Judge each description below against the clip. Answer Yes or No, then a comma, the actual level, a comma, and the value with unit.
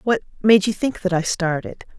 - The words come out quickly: Yes, fast, 210 wpm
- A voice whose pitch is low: No, high, 195 Hz